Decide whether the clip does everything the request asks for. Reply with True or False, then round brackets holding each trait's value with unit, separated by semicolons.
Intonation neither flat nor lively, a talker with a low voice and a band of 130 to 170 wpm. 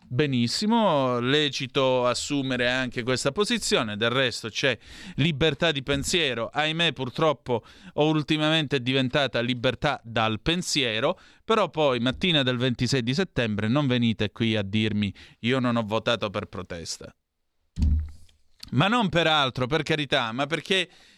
True (4.8 semitones; 130 Hz; 135 wpm)